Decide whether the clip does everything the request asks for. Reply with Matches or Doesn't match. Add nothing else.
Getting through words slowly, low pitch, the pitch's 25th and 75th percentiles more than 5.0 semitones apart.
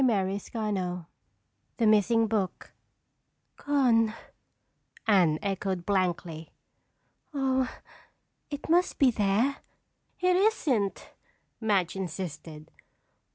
Doesn't match